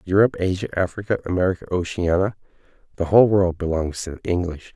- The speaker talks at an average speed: Yes, average, 150 wpm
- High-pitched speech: No, very low, 90 Hz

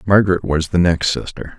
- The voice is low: Yes, very low, 85 Hz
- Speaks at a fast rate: No, average, 190 wpm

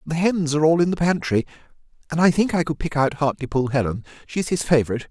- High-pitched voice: No, medium, 150 Hz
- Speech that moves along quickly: Yes, fast, 225 wpm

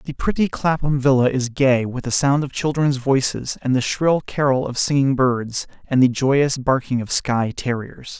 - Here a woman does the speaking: No, male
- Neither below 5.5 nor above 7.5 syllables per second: No, 4.5 syllables/s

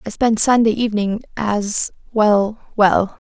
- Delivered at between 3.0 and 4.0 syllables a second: Yes, 3.9 syllables/s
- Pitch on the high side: Yes, high, 215 Hz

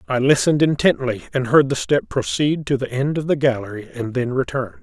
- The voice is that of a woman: No, male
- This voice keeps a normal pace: No, fast, 210 wpm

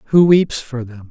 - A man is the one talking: Yes, male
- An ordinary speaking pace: No, fast, 220 wpm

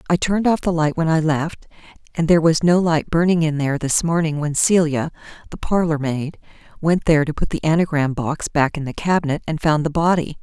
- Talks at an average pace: No, fast, 220 wpm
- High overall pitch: No, medium, 160 Hz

